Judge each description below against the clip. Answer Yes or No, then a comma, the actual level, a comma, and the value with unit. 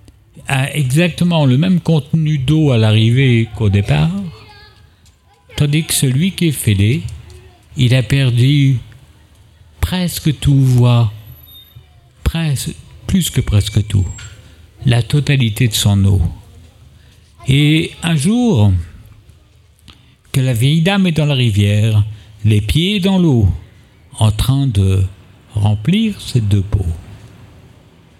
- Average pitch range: No, wide, 6.1 semitones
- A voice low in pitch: Yes, low, 115 Hz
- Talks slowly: Yes, slow, 115 wpm